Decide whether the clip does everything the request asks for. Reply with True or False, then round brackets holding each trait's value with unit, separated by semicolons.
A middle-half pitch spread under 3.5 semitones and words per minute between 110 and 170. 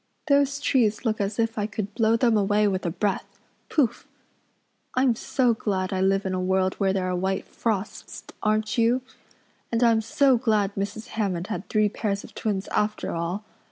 False (2.8 semitones; 185 wpm)